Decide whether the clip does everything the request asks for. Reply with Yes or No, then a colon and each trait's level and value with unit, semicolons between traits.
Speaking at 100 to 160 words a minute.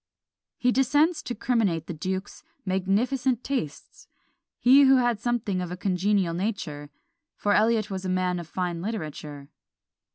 Yes: average, 140 wpm